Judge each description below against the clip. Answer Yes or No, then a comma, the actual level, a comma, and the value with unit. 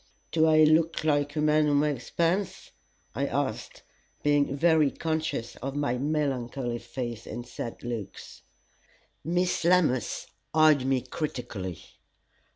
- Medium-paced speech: No, slow, 125 wpm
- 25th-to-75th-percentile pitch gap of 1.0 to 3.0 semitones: No, average, 4.2 semitones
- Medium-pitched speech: Yes, medium, 145 Hz